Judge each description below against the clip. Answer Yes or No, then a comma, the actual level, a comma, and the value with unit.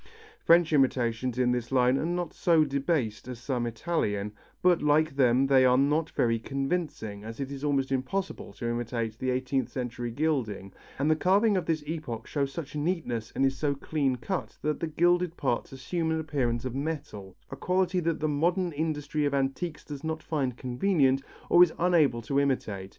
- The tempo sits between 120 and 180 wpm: No, average, 190 wpm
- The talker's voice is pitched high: No, medium, 140 Hz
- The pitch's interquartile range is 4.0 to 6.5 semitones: Yes, average, 4.4 semitones